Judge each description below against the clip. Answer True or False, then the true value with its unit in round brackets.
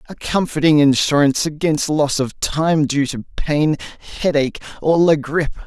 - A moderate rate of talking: True (150 wpm)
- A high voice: False (150 Hz)